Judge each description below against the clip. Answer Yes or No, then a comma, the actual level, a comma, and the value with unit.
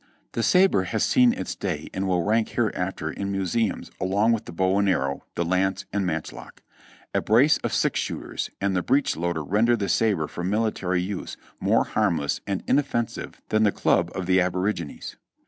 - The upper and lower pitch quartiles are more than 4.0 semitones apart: No, average, 3.5 semitones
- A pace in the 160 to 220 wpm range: Yes, average, 180 wpm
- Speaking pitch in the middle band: No, very low, 95 Hz